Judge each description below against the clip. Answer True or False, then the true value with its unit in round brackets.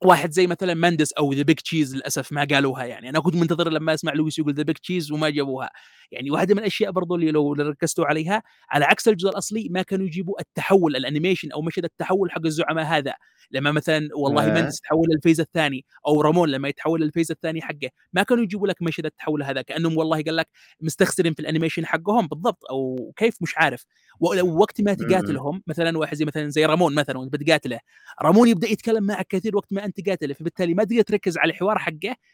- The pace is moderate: False (200 wpm)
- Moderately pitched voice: True (160 Hz)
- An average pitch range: True (3.6 semitones)